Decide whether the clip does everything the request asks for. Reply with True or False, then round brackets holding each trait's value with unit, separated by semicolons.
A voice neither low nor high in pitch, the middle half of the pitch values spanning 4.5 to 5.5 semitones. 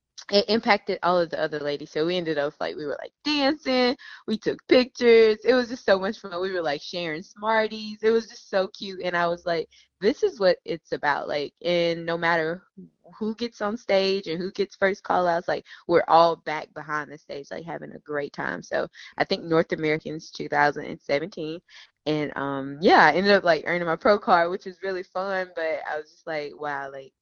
True (180 Hz; 5.1 semitones)